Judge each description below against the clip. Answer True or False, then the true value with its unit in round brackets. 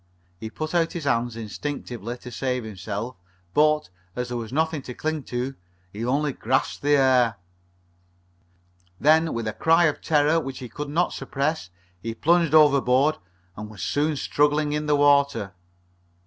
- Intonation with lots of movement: False (4.1 semitones)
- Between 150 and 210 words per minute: True (160 wpm)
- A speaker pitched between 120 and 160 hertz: True (140 Hz)